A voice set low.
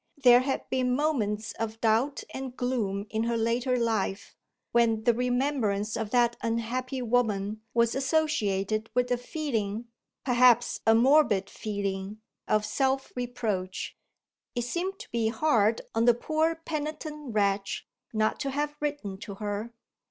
No: high, 235 Hz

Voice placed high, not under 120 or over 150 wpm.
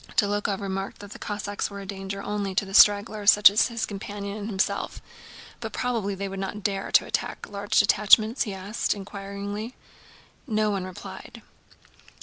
No: high, 205 Hz; average, 160 wpm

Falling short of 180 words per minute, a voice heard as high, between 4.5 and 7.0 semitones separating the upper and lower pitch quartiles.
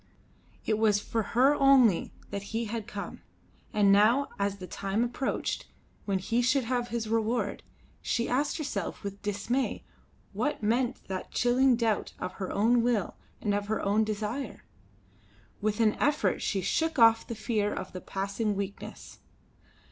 No: average, 155 wpm; high, 220 Hz; average, 3.2 semitones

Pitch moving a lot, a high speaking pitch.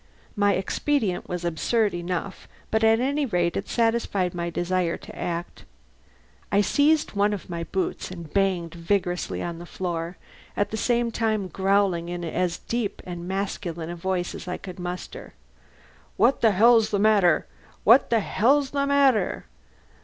No: average, 4.2 semitones; high, 195 Hz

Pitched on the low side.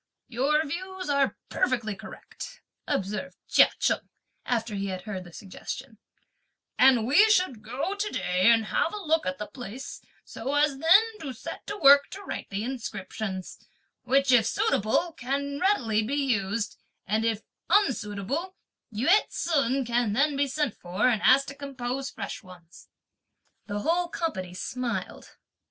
No: very high, 255 Hz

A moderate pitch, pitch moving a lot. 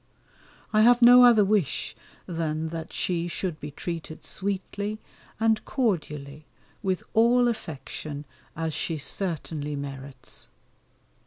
Yes: medium, 170 Hz; wide, 6.0 semitones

